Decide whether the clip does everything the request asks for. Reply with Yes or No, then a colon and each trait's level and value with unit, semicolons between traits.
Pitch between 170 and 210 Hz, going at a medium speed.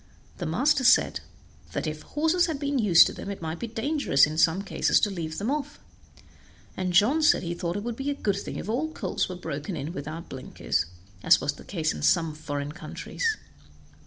No: high, 190 Hz; fast, 210 wpm